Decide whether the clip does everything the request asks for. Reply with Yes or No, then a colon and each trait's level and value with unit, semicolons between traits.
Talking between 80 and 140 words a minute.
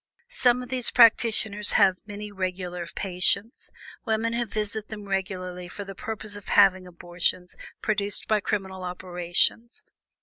Yes: slow, 135 wpm